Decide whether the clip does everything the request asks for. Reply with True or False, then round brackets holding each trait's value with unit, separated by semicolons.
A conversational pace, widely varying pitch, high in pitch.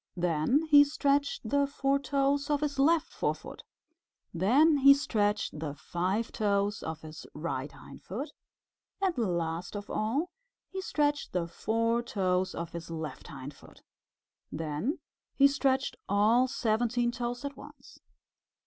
False (130 wpm; 8.3 semitones; 230 Hz)